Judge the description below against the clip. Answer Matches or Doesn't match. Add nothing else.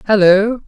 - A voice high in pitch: Matches